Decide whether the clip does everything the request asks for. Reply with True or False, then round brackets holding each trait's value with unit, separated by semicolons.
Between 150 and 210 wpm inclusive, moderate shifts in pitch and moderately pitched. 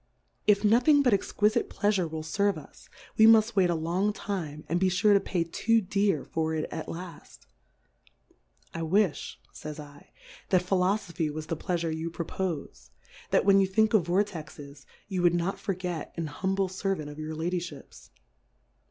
True (175 wpm; 4.0 semitones; 180 Hz)